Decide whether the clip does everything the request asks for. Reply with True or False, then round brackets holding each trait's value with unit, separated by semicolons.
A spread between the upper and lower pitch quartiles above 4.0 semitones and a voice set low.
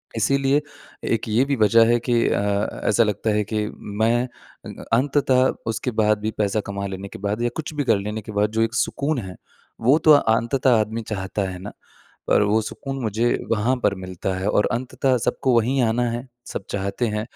False (3.3 semitones; 110 Hz)